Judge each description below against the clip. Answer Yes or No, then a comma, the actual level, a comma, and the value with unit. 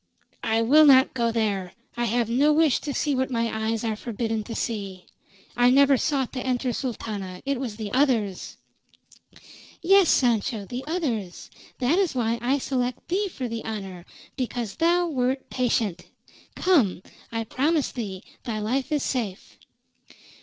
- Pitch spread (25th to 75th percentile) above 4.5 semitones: No, average, 3.9 semitones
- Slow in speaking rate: No, average, 155 wpm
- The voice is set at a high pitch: Yes, high, 245 Hz